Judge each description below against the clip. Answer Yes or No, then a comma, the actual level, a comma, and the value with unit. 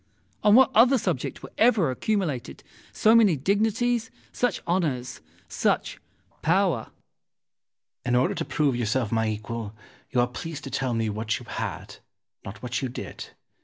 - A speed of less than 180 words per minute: Yes, average, 155 wpm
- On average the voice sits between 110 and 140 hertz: Yes, low, 135 Hz